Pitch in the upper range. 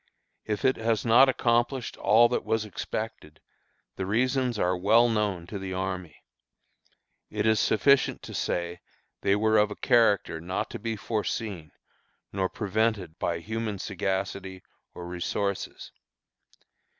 No: low, 105 Hz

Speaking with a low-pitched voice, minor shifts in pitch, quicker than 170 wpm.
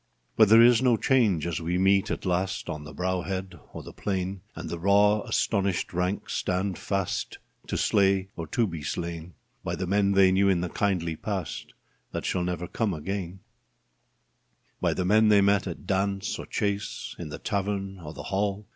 Yes: very low, 95 Hz; narrow, 2.2 semitones; average, 190 wpm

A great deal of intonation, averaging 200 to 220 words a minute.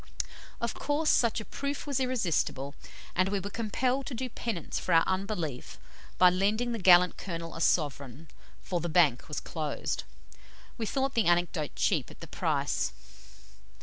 No: wide, 6.1 semitones; average, 160 wpm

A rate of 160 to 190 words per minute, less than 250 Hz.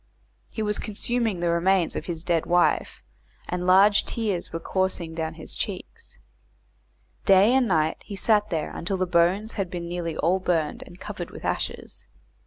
Yes: average, 170 wpm; medium, 185 Hz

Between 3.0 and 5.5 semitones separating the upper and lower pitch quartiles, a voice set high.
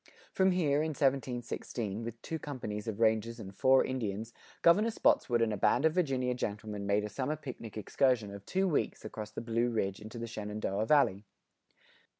No: average, 4.5 semitones; low, 115 Hz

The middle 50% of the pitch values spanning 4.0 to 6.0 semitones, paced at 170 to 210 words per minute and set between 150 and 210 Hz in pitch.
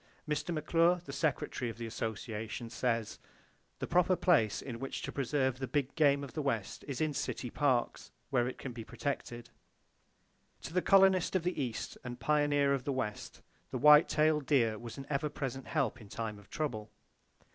No: average, 4.3 semitones; average, 190 wpm; low, 135 Hz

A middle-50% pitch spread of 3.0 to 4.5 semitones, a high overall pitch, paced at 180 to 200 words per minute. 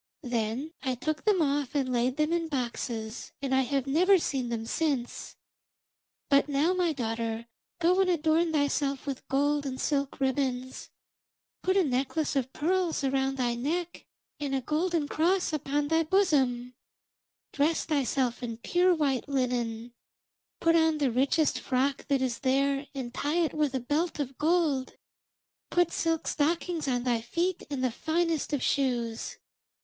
No: average, 4.0 semitones; very high, 280 Hz; average, 155 wpm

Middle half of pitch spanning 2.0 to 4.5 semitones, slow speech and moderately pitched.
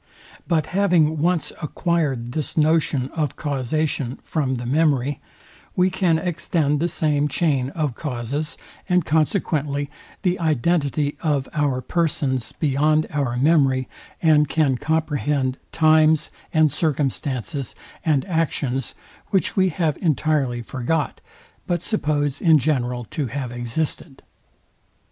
Yes: average, 3.1 semitones; slow, 115 wpm; medium, 150 Hz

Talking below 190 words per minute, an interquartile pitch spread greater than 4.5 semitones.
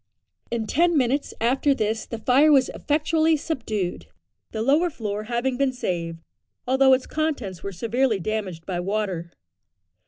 Yes: average, 145 wpm; average, 5.3 semitones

